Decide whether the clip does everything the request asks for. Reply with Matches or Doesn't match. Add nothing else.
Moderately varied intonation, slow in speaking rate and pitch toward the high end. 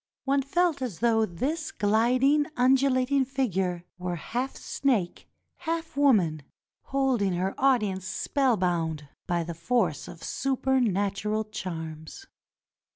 Doesn't match